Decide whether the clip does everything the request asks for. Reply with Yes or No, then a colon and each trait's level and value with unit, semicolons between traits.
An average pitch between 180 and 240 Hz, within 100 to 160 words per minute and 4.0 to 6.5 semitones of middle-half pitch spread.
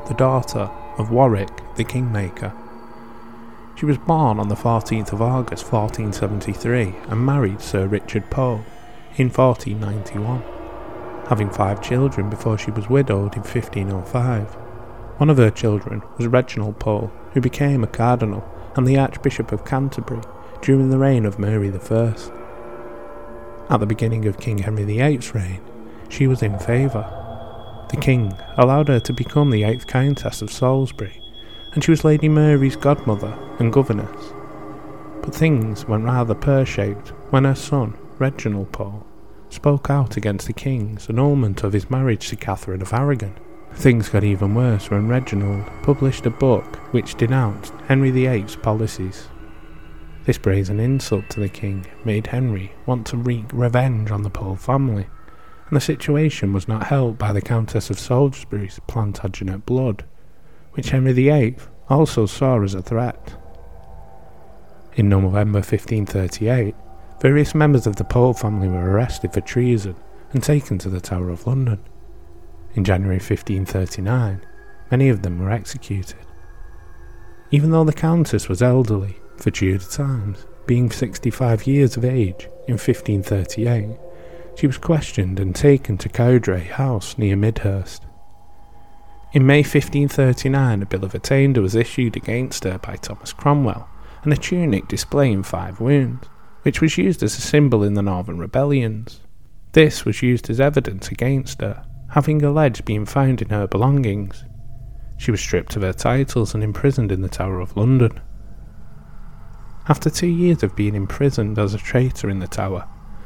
No: low, 115 Hz; average, 150 wpm; average, 4.4 semitones